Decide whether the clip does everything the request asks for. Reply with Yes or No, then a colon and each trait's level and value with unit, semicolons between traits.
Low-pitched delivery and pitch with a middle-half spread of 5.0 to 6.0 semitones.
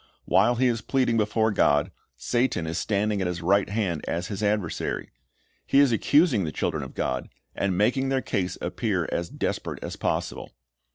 Yes: low, 105 Hz; average, 5.3 semitones